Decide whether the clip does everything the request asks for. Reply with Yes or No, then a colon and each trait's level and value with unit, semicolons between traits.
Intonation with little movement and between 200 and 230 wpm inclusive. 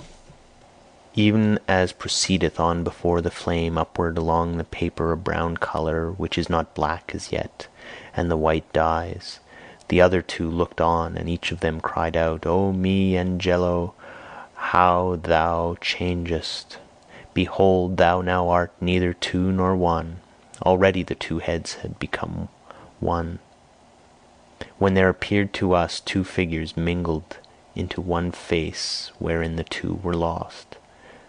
No: narrow, 1.6 semitones; average, 140 wpm